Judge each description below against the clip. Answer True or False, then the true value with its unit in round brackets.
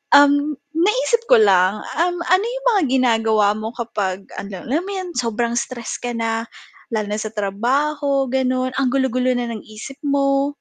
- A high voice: True (250 Hz)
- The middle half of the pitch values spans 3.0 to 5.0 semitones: True (4.6 semitones)